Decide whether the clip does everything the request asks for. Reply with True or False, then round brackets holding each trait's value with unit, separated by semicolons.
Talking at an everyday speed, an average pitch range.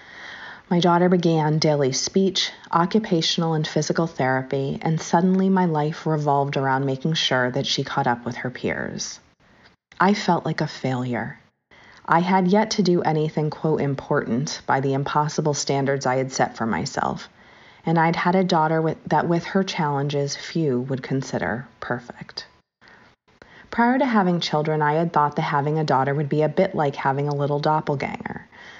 True (165 wpm; 3.6 semitones)